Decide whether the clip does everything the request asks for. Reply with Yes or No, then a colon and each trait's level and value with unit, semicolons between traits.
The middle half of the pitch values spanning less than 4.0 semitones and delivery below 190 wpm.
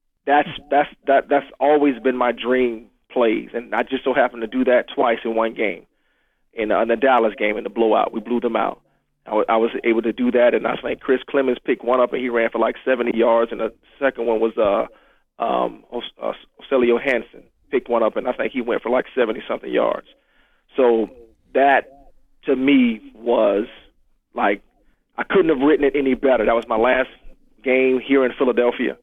No: narrow, 2.6 semitones; fast, 205 wpm